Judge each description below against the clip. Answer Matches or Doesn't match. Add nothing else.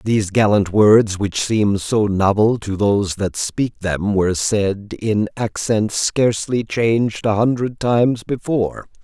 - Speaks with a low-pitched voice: Matches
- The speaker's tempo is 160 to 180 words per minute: Doesn't match